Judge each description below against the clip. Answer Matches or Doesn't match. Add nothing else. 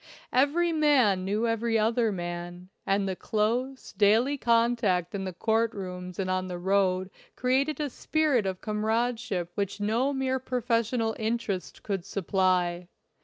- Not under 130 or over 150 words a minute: Matches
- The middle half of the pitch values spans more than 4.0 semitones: Matches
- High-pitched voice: Matches